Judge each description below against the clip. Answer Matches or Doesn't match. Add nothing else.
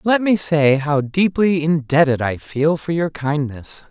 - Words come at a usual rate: Matches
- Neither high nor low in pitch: Matches